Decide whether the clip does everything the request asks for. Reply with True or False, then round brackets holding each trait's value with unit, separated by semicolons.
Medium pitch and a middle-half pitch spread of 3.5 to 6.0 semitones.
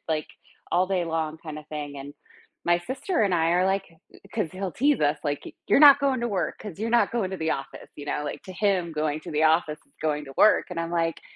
True (170 Hz; 4.4 semitones)